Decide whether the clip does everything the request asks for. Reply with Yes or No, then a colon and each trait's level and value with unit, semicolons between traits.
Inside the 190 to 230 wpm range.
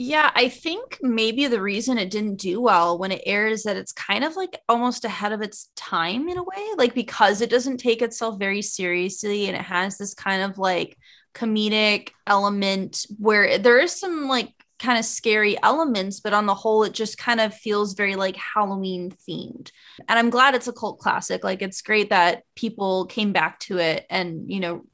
Yes: fast, 205 wpm